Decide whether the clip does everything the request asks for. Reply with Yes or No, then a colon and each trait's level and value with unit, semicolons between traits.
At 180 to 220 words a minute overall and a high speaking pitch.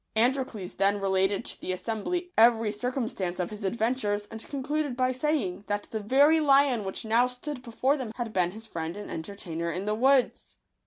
Yes: average, 190 wpm; high, 225 Hz